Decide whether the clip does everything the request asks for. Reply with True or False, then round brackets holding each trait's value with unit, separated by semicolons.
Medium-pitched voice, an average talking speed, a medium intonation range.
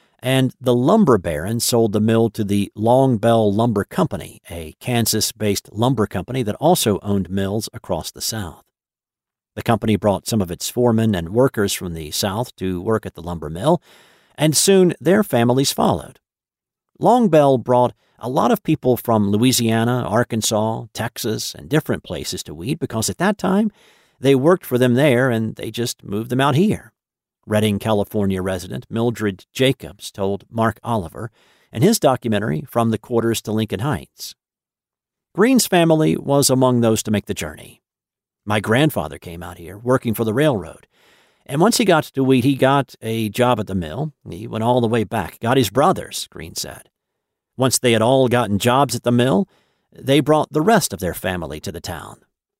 False (115 Hz; 175 wpm; 4.2 semitones)